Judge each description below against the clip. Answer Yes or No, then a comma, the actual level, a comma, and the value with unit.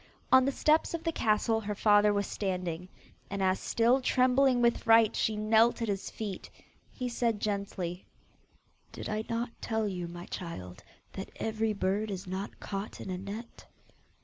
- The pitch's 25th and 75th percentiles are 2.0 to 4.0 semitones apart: Yes, average, 3.2 semitones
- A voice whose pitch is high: Yes, high, 210 Hz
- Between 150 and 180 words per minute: Yes, average, 170 wpm